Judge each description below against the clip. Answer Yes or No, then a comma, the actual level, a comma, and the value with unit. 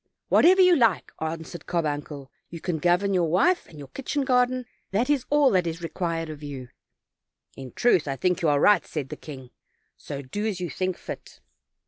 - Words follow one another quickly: No, average, 195 wpm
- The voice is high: No, medium, 175 Hz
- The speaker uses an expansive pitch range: Yes, wide, 7.0 semitones